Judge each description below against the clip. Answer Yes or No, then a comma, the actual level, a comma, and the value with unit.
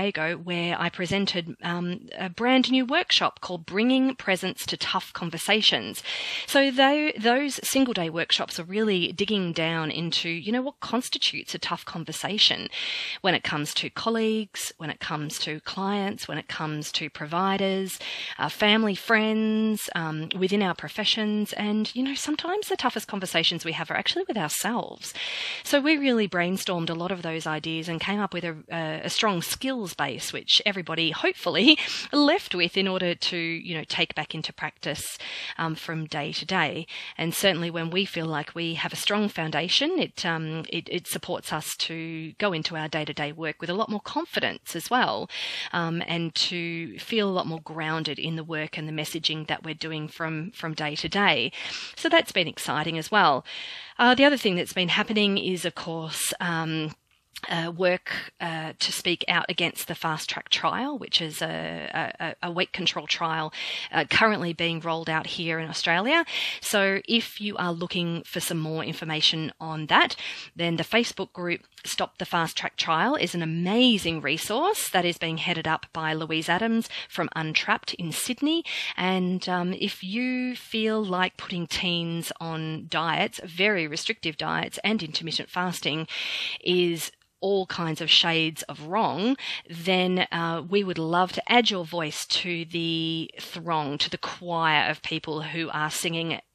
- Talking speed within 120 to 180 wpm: Yes, average, 175 wpm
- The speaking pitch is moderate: Yes, medium, 175 Hz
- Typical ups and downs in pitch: Yes, average, 4.2 semitones